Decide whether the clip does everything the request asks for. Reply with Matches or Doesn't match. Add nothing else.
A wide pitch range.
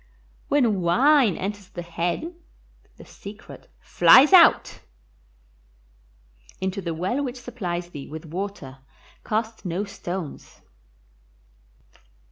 Matches